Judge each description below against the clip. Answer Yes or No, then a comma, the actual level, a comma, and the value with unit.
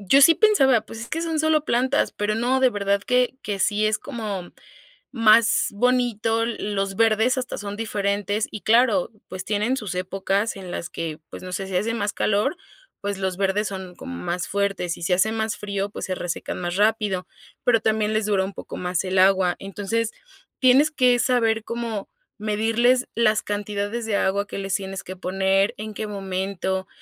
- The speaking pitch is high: Yes, high, 210 Hz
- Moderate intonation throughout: Yes, average, 3.0 semitones